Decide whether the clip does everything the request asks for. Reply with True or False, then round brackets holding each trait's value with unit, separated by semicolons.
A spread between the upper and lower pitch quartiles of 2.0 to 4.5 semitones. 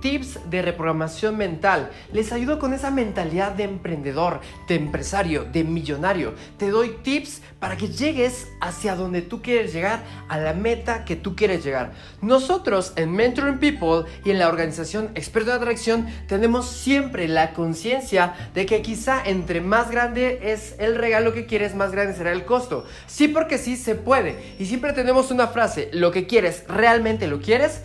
False (5.6 semitones)